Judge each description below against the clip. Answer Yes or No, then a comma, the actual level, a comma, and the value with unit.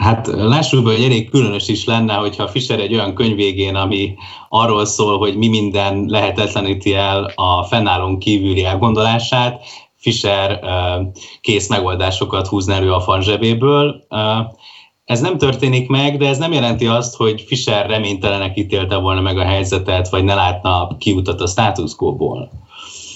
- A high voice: No, low, 105 Hz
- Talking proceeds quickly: No, average, 145 wpm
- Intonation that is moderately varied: Yes, average, 3.0 semitones